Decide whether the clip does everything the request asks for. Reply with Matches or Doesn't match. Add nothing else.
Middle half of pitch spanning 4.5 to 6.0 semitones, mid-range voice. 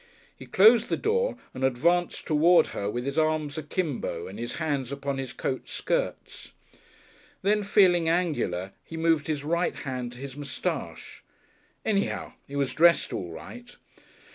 Matches